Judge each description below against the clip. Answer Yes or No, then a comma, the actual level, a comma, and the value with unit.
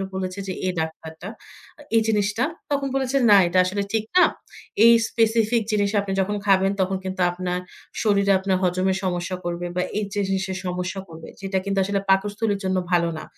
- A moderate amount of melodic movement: No, narrow, 2.1 semitones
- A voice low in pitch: No, high, 195 Hz